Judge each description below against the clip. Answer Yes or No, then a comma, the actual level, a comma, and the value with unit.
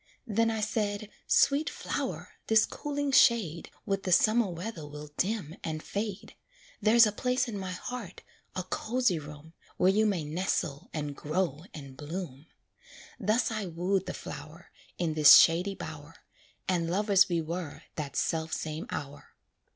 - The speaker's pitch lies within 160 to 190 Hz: Yes, medium, 185 Hz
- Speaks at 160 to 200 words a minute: No, average, 150 wpm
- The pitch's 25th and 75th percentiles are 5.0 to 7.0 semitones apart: Yes, average, 5.3 semitones